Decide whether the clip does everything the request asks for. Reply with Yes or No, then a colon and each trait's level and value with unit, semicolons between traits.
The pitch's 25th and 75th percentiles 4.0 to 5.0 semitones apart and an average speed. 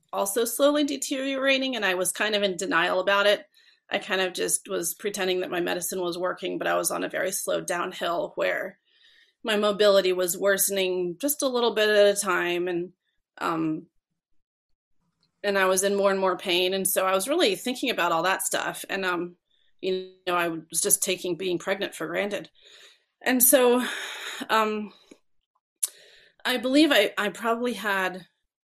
Yes: average, 4.4 semitones; average, 175 wpm